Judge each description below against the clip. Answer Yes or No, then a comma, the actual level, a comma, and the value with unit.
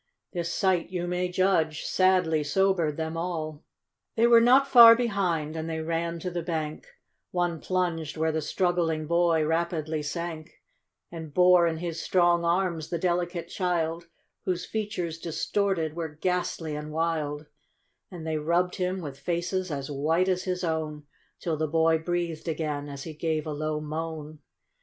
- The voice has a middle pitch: Yes, medium, 165 Hz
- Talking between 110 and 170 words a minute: Yes, average, 160 wpm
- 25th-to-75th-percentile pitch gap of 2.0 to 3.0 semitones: Yes, narrow, 2.4 semitones